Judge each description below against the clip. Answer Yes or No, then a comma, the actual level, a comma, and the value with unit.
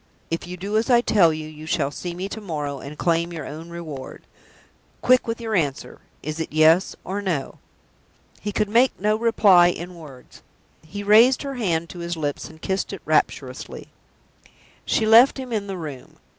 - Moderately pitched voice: Yes, medium, 175 Hz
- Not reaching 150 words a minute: No, average, 185 wpm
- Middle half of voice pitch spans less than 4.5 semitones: No, average, 5.2 semitones